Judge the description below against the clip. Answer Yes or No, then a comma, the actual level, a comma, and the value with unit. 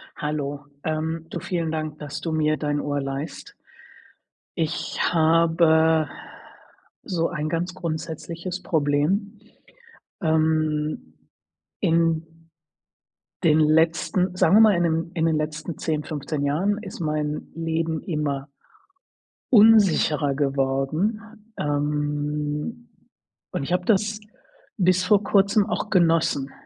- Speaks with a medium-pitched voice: Yes, medium, 160 Hz